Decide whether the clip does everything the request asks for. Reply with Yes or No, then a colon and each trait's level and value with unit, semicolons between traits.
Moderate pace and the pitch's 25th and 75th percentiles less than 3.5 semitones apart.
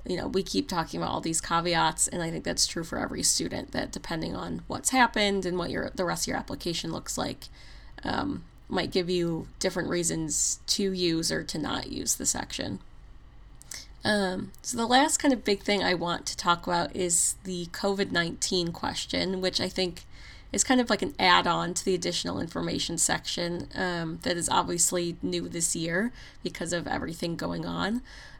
Yes: average, 190 wpm; average, 2.7 semitones